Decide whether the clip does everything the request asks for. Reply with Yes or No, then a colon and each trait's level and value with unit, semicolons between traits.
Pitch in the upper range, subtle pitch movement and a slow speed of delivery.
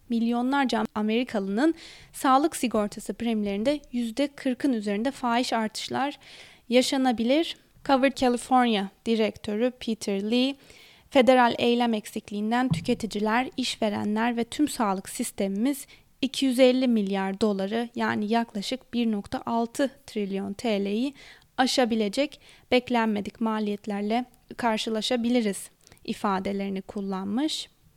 No: high, 235 Hz; average, 3.3 semitones; slow, 80 wpm